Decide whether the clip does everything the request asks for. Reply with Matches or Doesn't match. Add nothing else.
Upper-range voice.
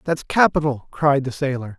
Doesn't match